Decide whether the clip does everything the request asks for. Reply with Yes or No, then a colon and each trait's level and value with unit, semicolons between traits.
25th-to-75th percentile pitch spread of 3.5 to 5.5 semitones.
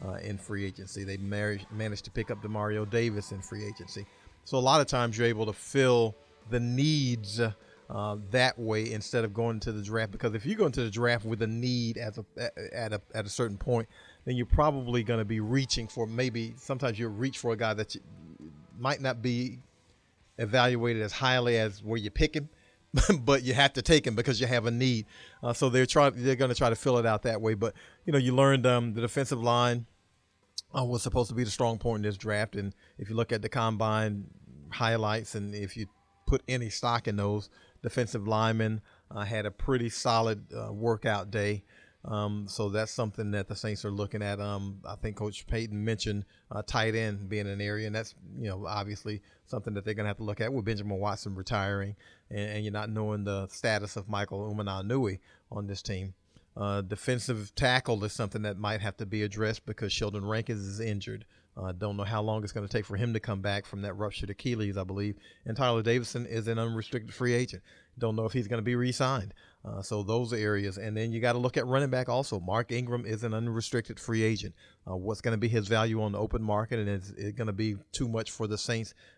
No: narrow, 2.6 semitones